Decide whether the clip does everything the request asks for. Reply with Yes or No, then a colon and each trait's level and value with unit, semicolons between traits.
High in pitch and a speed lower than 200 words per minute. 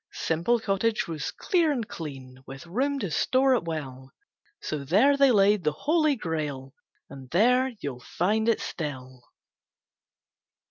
No: medium, 175 Hz; average, 140 wpm